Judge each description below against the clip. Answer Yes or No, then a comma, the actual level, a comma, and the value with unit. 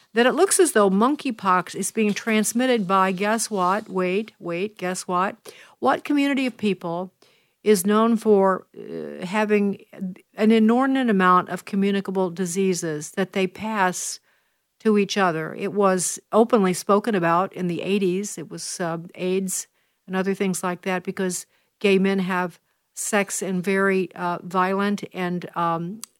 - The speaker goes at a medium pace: Yes, average, 150 wpm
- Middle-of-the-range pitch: No, high, 195 Hz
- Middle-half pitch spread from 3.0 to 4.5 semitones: No, narrow, 2.6 semitones